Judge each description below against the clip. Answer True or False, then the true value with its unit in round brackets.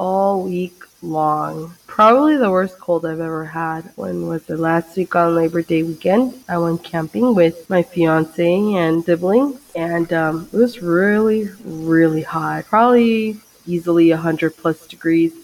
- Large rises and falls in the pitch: False (4.1 semitones)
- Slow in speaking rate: False (155 wpm)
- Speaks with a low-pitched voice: False (170 Hz)